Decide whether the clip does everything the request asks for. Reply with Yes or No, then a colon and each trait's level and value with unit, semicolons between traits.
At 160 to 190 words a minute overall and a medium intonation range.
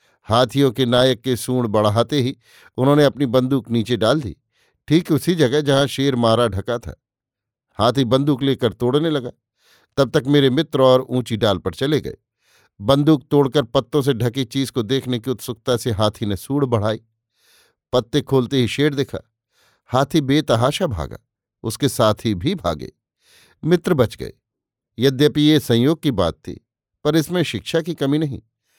Yes: average, 165 wpm; average, 3.5 semitones